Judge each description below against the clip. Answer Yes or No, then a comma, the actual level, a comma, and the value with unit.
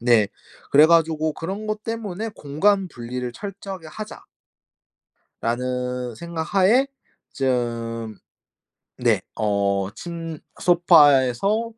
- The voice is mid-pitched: Yes, medium, 155 Hz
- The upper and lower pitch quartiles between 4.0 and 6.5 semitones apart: No, wide, 7.8 semitones